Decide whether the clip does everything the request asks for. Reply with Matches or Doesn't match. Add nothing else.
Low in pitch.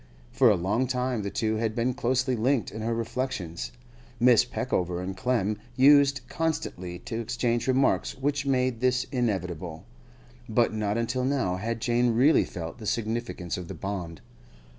Matches